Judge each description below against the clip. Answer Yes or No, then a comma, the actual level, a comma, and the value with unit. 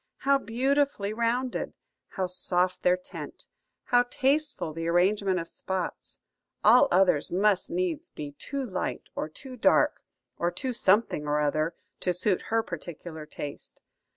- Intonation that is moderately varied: No, wide, 6.3 semitones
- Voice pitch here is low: No, high, 190 Hz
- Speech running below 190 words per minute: Yes, average, 140 wpm